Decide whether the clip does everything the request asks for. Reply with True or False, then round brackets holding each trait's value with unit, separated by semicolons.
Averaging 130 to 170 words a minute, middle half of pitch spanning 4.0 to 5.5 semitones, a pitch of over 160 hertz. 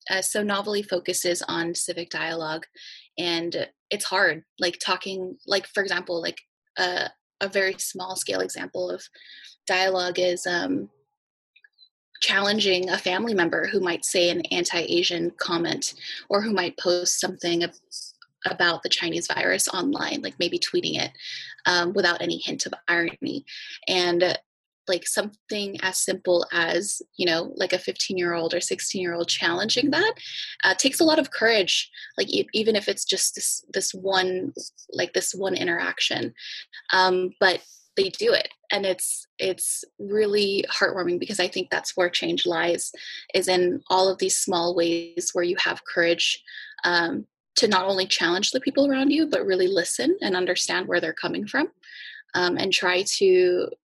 True (155 wpm; 4.3 semitones; 190 Hz)